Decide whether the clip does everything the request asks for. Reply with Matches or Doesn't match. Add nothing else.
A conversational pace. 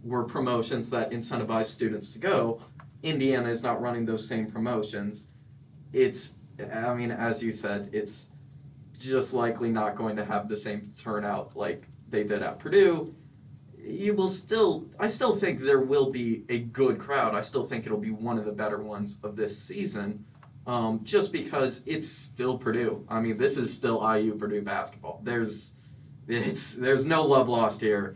Matches